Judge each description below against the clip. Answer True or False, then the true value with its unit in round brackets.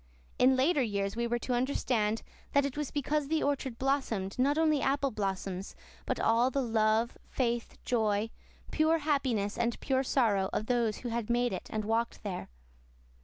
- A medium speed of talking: True (170 wpm)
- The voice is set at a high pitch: True (240 Hz)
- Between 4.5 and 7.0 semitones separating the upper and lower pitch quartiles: False (4.0 semitones)